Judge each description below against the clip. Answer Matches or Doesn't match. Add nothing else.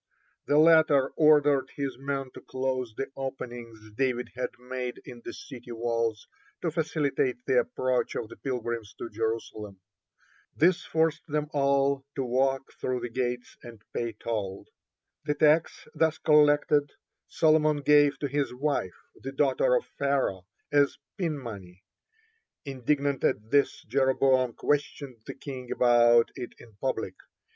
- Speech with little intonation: Doesn't match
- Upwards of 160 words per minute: Doesn't match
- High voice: Doesn't match